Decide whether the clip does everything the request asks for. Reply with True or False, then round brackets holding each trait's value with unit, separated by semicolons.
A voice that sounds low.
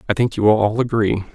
True (110 Hz)